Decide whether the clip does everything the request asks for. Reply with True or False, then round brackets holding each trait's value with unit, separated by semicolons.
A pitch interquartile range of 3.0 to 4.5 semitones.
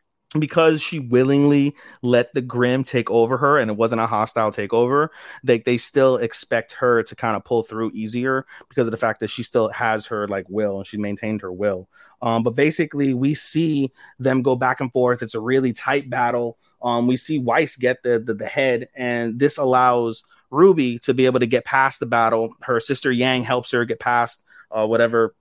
False (2.6 semitones)